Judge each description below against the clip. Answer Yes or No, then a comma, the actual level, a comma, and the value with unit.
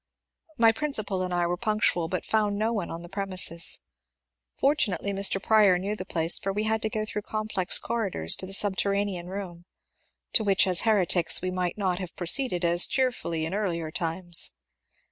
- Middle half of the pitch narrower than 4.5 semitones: Yes, average, 3.4 semitones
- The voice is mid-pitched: No, high, 195 Hz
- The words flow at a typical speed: Yes, average, 185 wpm